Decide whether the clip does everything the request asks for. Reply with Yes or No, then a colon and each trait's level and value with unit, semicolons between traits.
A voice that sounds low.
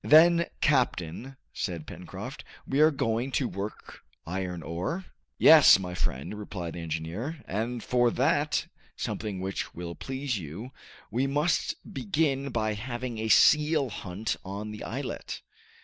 Yes: low, 115 Hz